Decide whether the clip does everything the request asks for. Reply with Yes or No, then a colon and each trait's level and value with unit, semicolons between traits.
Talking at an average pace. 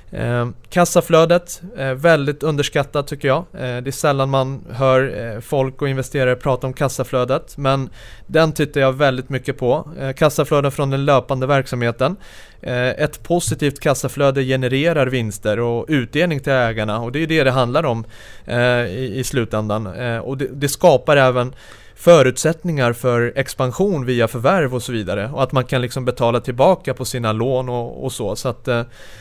Yes: average, 175 wpm